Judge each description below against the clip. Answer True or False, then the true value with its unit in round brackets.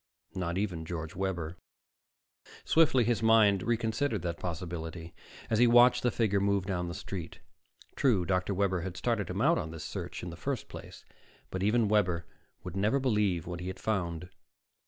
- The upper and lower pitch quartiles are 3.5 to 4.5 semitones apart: True (4.2 semitones)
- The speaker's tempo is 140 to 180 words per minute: True (175 wpm)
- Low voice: True (95 Hz)